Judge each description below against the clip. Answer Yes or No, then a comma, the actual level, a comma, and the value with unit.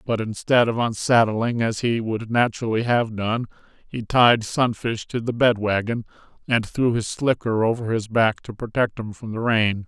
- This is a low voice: Yes, low, 115 Hz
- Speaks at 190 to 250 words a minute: No, average, 180 wpm